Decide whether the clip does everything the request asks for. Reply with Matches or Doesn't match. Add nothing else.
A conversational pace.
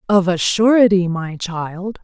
Matches